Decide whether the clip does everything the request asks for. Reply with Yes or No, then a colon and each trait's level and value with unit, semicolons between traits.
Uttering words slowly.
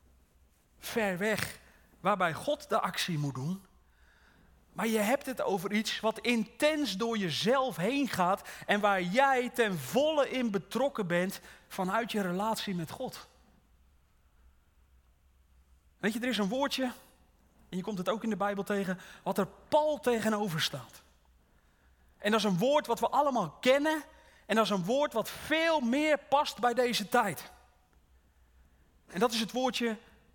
No: average, 155 wpm